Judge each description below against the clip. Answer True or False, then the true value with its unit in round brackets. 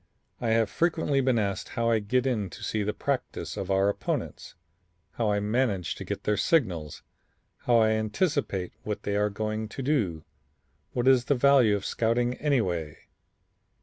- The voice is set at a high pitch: False (110 Hz)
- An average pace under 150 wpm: False (170 wpm)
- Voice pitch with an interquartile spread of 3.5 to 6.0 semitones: True (3.9 semitones)